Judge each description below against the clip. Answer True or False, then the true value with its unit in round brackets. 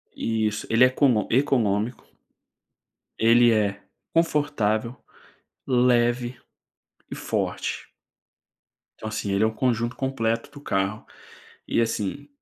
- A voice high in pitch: False (115 Hz)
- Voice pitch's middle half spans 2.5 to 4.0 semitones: True (2.8 semitones)